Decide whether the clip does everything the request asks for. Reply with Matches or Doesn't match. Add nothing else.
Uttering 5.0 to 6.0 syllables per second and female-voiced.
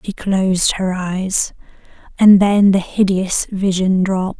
Matches